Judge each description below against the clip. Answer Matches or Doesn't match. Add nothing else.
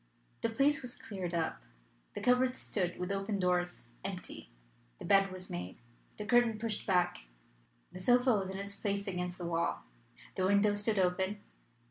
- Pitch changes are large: Doesn't match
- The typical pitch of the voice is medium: Doesn't match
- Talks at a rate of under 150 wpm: Doesn't match